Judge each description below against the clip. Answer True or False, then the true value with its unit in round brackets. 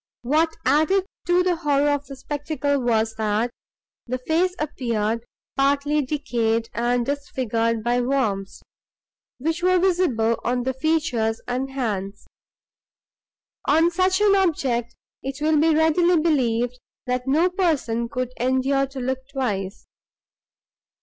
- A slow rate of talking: True (125 wpm)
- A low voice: False (270 Hz)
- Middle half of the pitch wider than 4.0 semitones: True (4.8 semitones)